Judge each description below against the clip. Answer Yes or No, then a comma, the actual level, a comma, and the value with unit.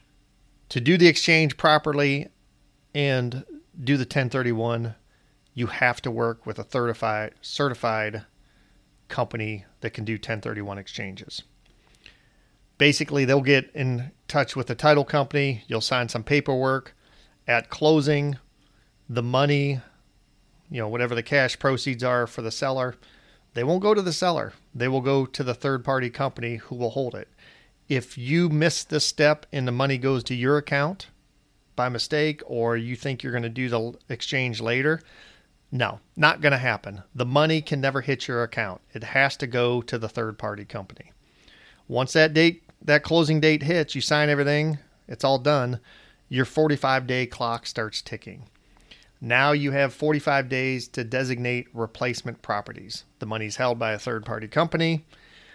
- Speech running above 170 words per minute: No, average, 155 wpm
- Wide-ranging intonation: No, average, 3.6 semitones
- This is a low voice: Yes, low, 130 Hz